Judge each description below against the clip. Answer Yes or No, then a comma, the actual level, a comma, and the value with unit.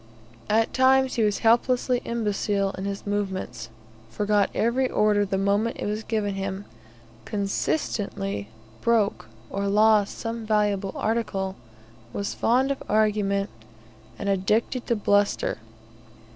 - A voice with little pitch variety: Yes, narrow, 2.3 semitones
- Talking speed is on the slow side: Yes, slow, 120 wpm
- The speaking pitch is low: No, high, 210 Hz